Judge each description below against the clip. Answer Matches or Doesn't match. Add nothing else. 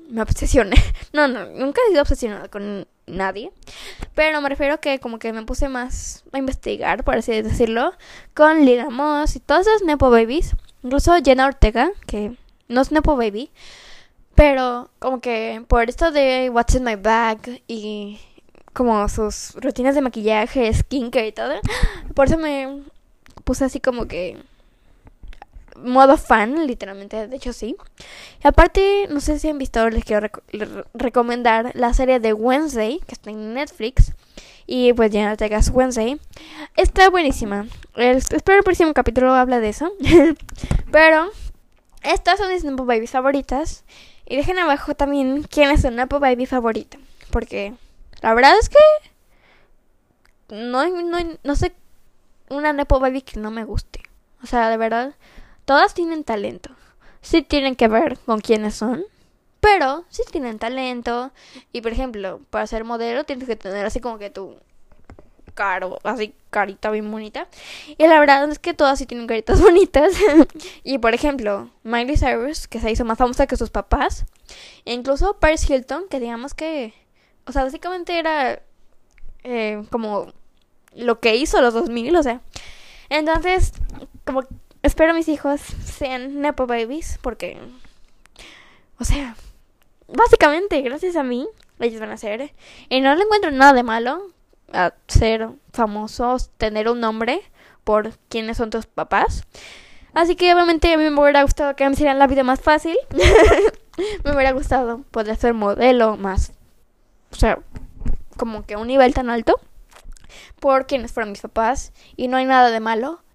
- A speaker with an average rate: Matches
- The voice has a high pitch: Matches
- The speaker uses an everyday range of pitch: Matches